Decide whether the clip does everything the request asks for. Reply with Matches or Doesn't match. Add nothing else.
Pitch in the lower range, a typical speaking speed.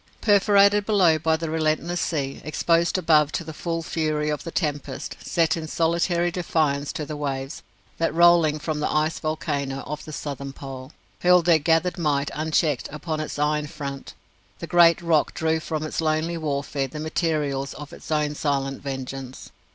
Doesn't match